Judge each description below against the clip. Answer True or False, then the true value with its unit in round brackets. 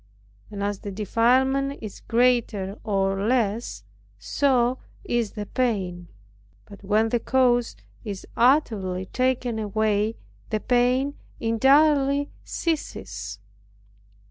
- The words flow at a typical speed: False (100 wpm)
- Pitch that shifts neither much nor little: True (4.1 semitones)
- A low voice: False (225 Hz)